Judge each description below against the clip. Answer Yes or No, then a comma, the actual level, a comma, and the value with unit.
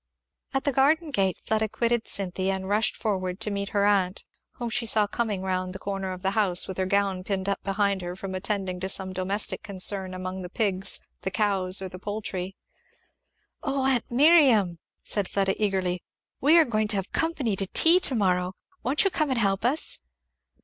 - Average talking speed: Yes, average, 195 wpm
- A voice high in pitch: Yes, high, 200 Hz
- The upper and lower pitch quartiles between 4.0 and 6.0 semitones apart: No, average, 3.2 semitones